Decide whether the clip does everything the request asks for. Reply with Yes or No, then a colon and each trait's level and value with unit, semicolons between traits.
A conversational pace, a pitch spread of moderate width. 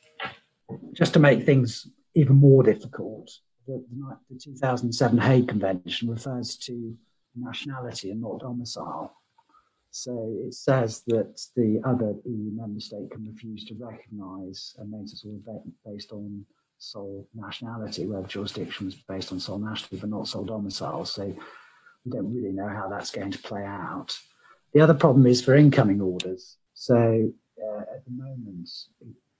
Yes: average, 160 wpm; average, 3.9 semitones